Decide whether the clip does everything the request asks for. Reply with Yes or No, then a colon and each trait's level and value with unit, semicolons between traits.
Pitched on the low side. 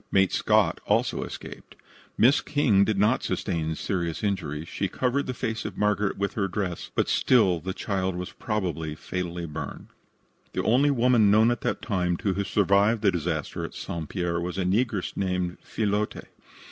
Yes: low, 100 Hz